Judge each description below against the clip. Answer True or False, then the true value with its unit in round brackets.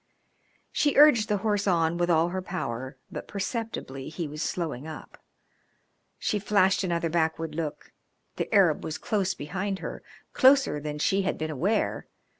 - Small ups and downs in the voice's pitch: False (4.4 semitones)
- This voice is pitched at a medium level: True (175 Hz)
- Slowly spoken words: False (155 wpm)